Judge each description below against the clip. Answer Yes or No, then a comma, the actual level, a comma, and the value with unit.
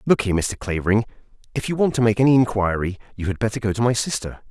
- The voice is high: No, low, 110 Hz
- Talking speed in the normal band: No, fast, 240 wpm